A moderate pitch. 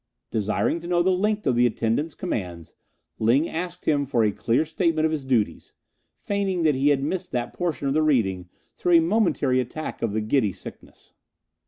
Yes: medium, 145 Hz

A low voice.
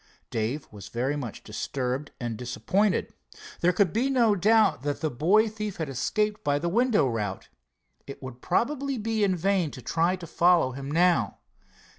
No: medium, 165 Hz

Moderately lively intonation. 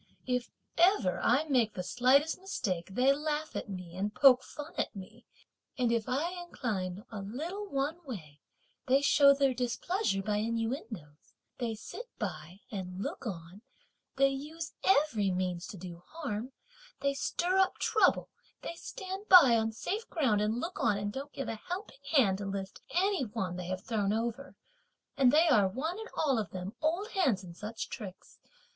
No: wide, 7.1 semitones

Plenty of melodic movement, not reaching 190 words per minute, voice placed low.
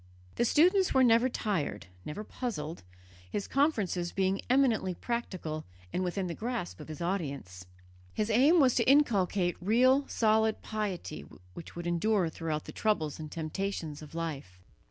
No: wide, 6.3 semitones; average, 150 wpm; high, 195 Hz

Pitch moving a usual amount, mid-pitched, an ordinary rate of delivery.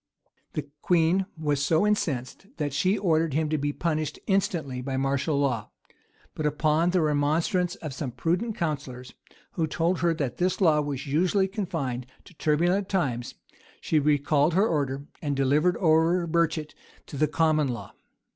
Yes: average, 3.4 semitones; medium, 155 Hz; average, 155 wpm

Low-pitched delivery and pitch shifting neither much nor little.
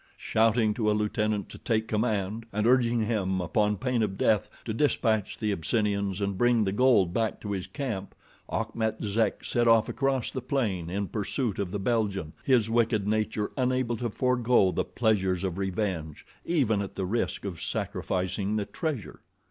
Yes: low, 105 Hz; average, 3.0 semitones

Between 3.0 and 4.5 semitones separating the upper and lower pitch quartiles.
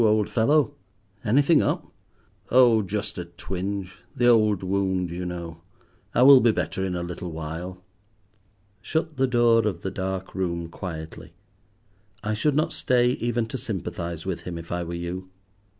No: average, 5.2 semitones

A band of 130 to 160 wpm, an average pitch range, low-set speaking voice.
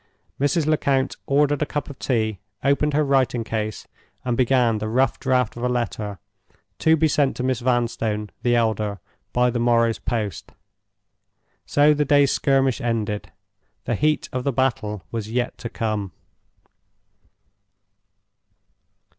Yes: average, 140 wpm; average, 3.7 semitones; low, 125 Hz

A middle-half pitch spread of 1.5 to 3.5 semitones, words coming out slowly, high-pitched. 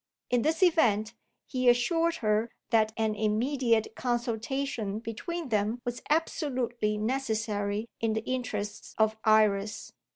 Yes: average, 3.1 semitones; slow, 120 wpm; high, 225 Hz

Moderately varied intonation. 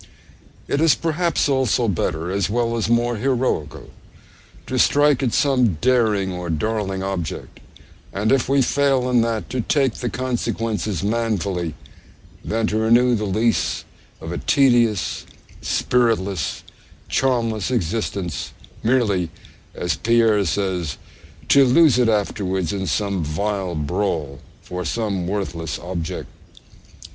Yes: average, 4.8 semitones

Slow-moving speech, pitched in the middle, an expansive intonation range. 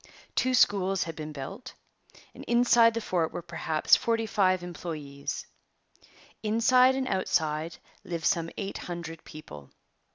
Yes: slow, 125 wpm; medium, 180 Hz; wide, 5.9 semitones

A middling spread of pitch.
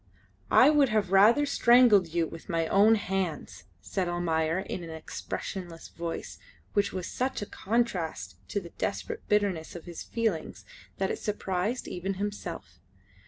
Yes: average, 3.9 semitones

